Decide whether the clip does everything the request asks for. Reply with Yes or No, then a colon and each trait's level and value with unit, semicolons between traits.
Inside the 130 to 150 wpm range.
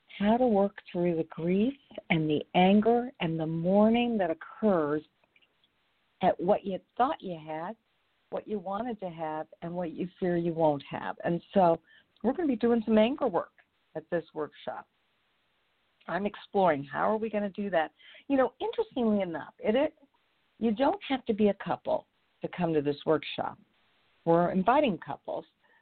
No: average, 175 wpm